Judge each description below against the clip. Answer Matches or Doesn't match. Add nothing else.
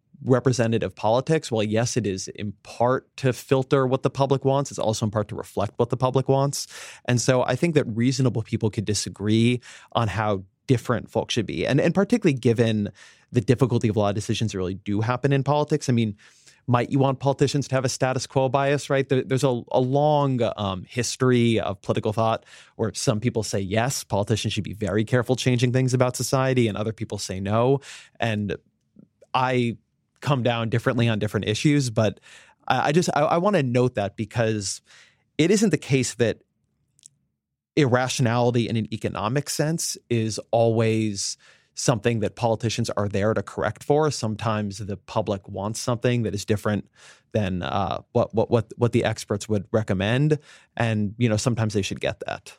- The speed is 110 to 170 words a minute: Doesn't match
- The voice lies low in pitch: Matches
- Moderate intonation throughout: Matches